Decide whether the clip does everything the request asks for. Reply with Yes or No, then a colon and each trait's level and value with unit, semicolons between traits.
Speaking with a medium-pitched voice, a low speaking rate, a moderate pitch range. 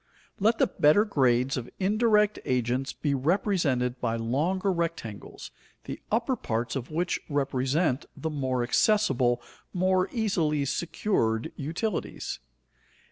No: medium, 150 Hz; slow, 115 wpm; wide, 7.1 semitones